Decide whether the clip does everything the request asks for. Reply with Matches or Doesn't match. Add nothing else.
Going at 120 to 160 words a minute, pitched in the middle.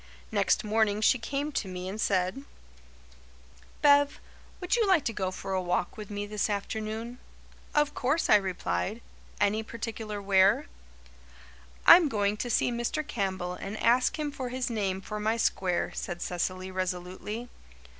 Doesn't match